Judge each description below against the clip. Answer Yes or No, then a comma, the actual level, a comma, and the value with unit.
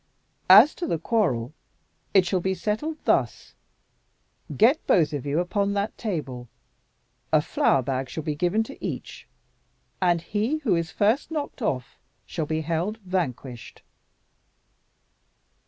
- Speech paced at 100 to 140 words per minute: Yes, slow, 135 wpm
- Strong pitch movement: Yes, wide, 6.1 semitones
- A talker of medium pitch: Yes, medium, 180 Hz